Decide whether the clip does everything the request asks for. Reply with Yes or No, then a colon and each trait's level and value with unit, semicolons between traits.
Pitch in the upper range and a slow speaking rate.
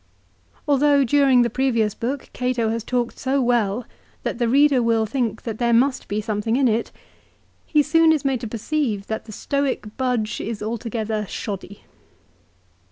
No: high, 235 Hz; average, 165 wpm